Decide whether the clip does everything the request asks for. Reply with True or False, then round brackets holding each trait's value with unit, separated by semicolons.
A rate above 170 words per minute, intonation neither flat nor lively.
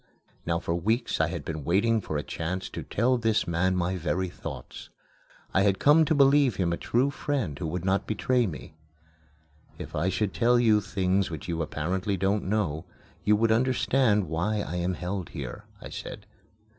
True (185 wpm; 4.7 semitones)